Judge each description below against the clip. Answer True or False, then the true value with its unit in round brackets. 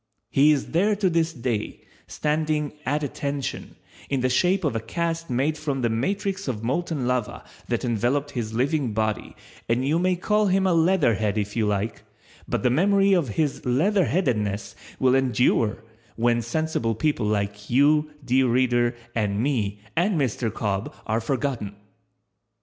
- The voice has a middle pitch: False (130 Hz)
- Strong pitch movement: True (5.8 semitones)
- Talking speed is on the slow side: False (155 wpm)